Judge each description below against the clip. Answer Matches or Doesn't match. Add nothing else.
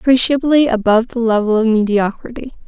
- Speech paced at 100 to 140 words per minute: Matches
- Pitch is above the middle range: Matches